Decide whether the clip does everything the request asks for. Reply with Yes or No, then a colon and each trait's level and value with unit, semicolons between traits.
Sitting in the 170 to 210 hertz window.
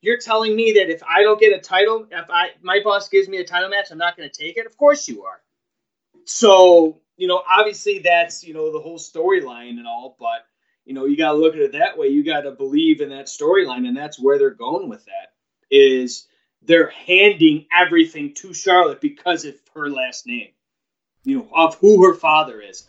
Yes: medium, 185 Hz